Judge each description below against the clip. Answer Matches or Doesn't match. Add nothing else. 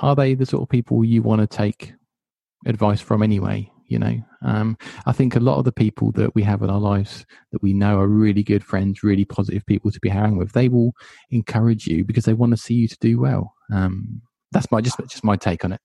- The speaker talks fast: Matches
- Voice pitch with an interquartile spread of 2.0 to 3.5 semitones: Matches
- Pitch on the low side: Matches